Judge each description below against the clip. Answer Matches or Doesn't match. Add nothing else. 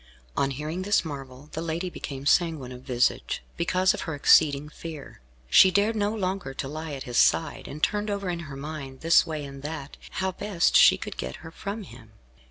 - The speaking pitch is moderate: Matches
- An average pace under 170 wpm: Doesn't match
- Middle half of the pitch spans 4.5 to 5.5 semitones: Matches